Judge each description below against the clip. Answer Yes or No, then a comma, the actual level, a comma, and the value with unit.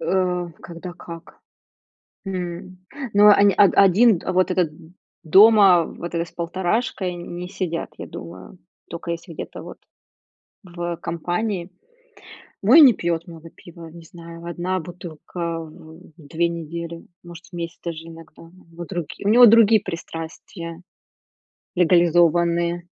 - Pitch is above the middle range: No, medium, 175 Hz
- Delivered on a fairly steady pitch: Yes, narrow, 1.7 semitones